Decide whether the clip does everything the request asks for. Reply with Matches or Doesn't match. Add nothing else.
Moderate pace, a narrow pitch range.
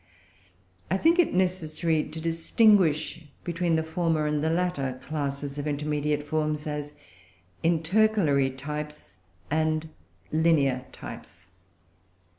Doesn't match